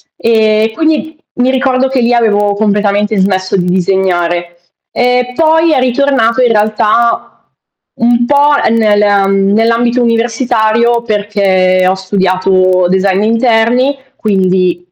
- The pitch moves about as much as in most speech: Yes, average, 4.0 semitones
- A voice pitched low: No, high, 220 Hz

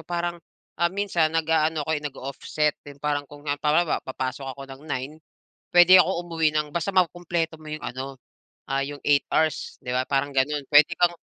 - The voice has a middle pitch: Yes, medium, 150 Hz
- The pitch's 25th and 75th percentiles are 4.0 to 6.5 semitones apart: No, average, 3.2 semitones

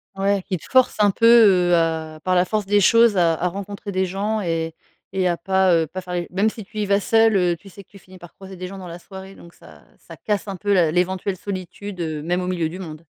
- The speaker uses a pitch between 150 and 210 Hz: Yes, medium, 185 Hz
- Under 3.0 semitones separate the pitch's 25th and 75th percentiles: Yes, narrow, 2.5 semitones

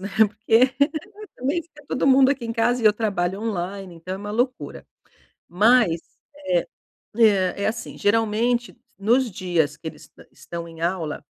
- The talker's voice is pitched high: Yes, high, 215 Hz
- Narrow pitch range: No, average, 4.7 semitones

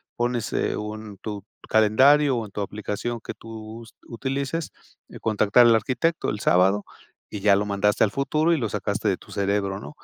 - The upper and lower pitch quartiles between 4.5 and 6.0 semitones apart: No, average, 3.1 semitones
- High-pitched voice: No, low, 110 Hz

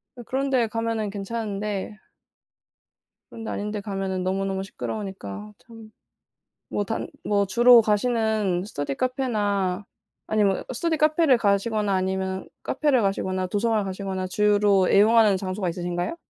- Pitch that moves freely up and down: No, average, 3.0 semitones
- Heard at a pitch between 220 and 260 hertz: No, high, 205 Hz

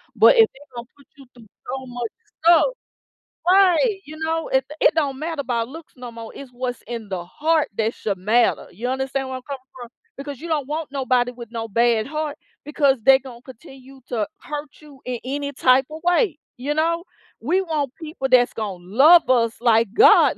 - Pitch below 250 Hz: No, very high, 265 Hz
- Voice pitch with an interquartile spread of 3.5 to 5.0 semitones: Yes, average, 4.1 semitones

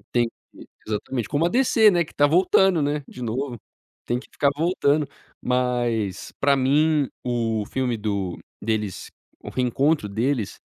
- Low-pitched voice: Yes, low, 130 Hz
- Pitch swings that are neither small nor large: Yes, average, 4.7 semitones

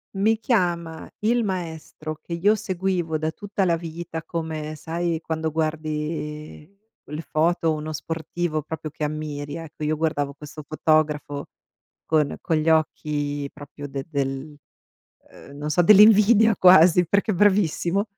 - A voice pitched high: No, medium, 160 Hz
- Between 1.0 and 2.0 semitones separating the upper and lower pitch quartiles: No, narrow, 2.6 semitones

